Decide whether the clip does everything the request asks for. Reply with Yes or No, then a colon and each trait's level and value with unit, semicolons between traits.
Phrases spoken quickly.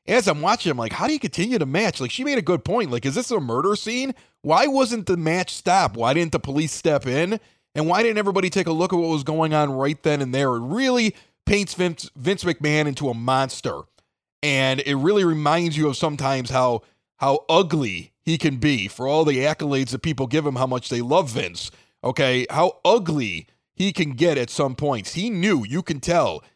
Yes: fast, 225 wpm